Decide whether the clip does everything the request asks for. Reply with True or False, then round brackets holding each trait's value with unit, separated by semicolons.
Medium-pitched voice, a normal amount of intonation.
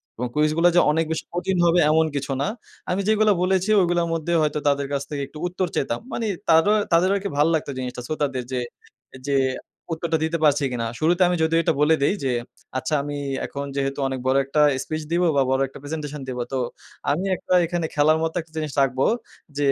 True (155 Hz; 3.3 semitones)